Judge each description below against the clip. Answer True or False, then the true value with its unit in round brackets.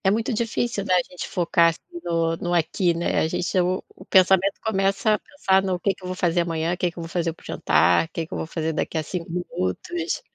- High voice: False (180 Hz)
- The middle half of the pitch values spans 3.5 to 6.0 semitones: False (2.5 semitones)